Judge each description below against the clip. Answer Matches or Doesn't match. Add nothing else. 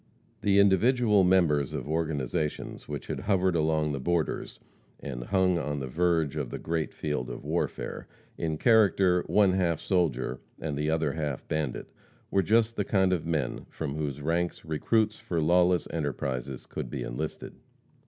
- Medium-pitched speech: Doesn't match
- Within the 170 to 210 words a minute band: Doesn't match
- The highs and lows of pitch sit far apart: Doesn't match